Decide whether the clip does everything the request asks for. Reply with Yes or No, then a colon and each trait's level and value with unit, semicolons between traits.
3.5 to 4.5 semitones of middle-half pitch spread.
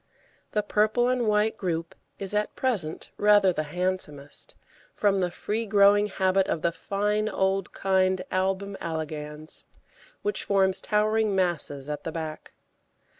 Yes: average, 3.8 semitones